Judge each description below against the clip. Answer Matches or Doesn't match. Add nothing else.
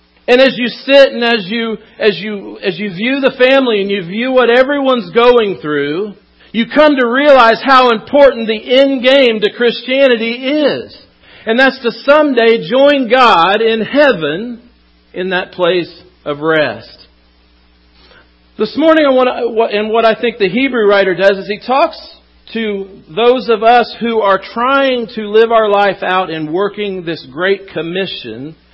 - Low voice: Doesn't match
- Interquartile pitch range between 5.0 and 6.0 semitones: Doesn't match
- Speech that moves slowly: Doesn't match